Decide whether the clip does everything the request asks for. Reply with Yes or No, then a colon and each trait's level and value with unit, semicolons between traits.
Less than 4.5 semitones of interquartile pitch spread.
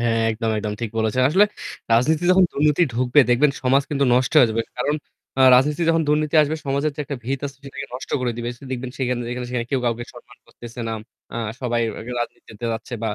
Yes: average, 3.4 semitones